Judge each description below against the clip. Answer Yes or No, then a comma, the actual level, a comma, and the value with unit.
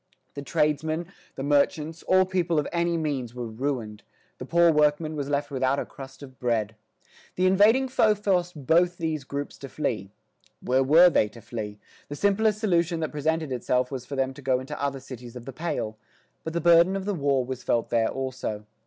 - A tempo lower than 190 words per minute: No, average, 195 wpm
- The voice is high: No, medium, 145 Hz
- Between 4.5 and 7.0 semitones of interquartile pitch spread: Yes, average, 4.8 semitones